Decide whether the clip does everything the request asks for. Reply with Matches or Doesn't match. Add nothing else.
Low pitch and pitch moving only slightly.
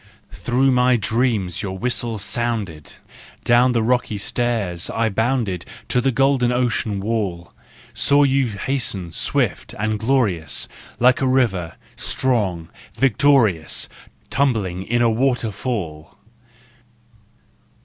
Doesn't match